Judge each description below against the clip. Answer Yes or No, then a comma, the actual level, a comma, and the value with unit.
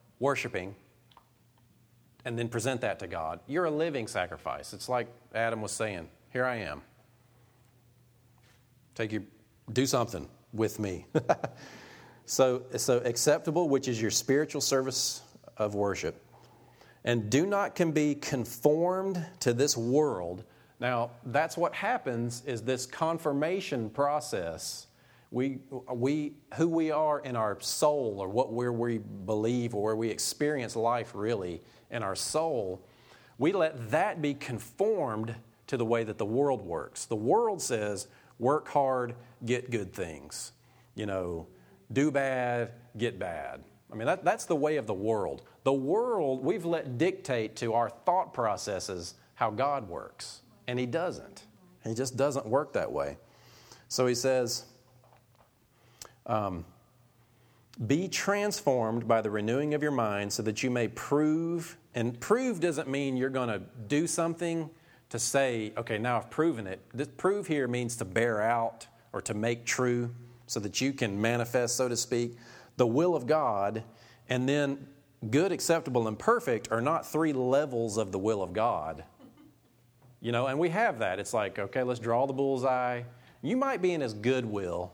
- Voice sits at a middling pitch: No, low, 125 Hz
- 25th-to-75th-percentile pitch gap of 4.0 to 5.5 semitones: No, average, 3.4 semitones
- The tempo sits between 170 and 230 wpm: No, average, 155 wpm